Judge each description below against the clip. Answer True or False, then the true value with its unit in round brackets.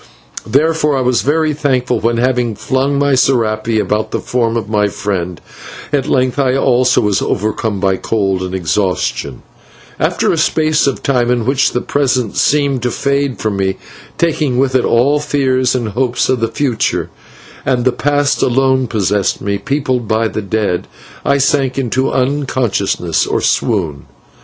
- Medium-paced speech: True (165 wpm)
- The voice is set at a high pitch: False (125 Hz)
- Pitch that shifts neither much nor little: True (4.1 semitones)